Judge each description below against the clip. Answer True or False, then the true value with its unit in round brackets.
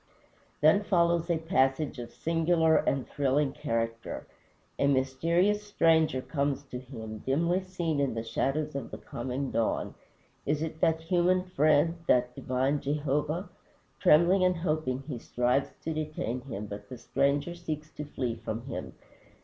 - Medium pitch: True (145 Hz)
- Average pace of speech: True (150 wpm)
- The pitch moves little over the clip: False (4.1 semitones)